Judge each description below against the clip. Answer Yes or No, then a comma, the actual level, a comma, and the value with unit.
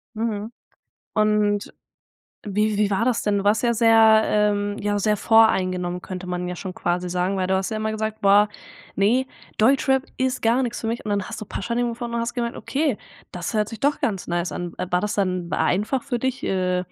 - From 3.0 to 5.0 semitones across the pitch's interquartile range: Yes, average, 3.4 semitones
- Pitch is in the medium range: No, high, 210 Hz